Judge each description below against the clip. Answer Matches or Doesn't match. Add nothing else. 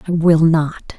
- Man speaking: Doesn't match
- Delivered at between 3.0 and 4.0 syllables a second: Matches